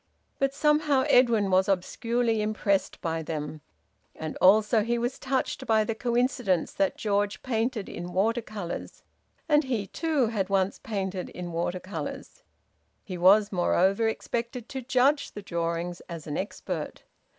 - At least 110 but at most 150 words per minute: Yes, average, 145 wpm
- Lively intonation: No, average, 4.8 semitones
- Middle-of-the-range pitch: No, high, 215 Hz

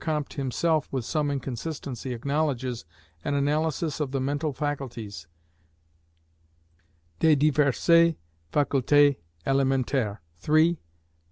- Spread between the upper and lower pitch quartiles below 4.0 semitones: Yes, narrow, 2.6 semitones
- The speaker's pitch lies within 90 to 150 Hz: Yes, medium, 140 Hz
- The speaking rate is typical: No, slow, 90 wpm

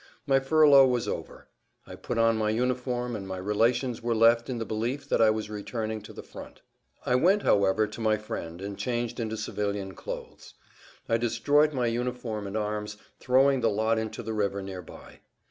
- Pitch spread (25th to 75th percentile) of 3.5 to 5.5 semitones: No, average, 2.8 semitones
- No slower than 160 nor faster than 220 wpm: Yes, average, 190 wpm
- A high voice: No, low, 115 Hz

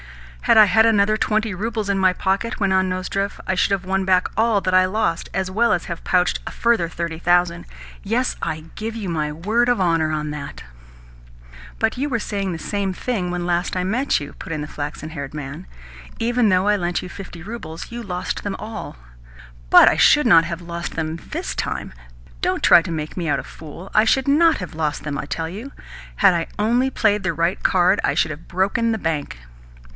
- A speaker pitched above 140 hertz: Yes, medium, 185 Hz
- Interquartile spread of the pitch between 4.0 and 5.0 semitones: Yes, average, 4.5 semitones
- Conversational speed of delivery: No, fast, 220 wpm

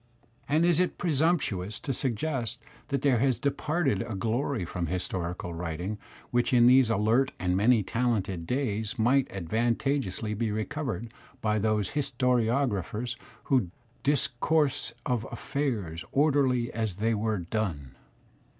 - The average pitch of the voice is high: No, low, 115 Hz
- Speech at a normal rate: No, slow, 125 wpm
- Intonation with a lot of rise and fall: No, average, 4.8 semitones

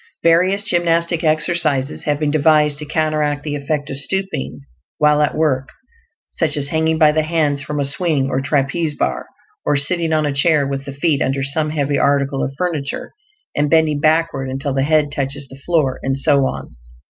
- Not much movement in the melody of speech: Yes, narrow, 2.3 semitones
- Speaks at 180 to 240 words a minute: Yes, average, 185 wpm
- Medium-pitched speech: Yes, medium, 150 Hz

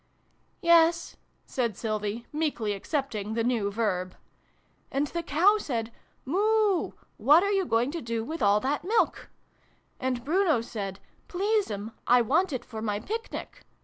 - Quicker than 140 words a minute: Yes, average, 165 wpm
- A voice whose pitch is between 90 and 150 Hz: No, very high, 255 Hz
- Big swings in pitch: Yes, wide, 7.5 semitones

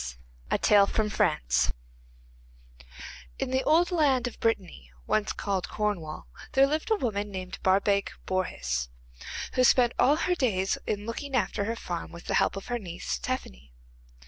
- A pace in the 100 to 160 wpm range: Yes, average, 150 wpm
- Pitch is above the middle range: Yes, high, 205 Hz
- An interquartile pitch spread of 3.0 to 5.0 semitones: No, wide, 5.5 semitones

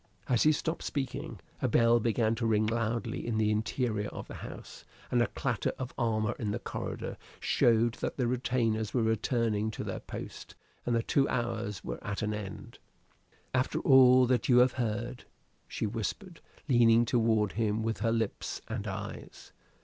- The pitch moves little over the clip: Yes, narrow, 2.1 semitones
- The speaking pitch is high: No, low, 115 Hz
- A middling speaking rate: Yes, average, 170 wpm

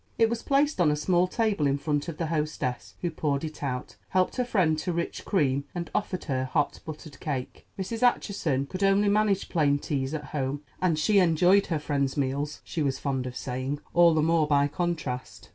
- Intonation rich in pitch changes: No, average, 4.5 semitones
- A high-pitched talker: No, medium, 155 Hz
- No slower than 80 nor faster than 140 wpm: No, fast, 205 wpm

